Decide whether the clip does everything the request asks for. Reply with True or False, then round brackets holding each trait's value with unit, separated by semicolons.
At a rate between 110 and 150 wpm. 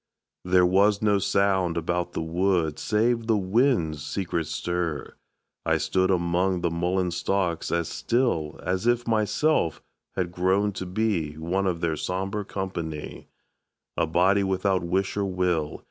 True (145 wpm)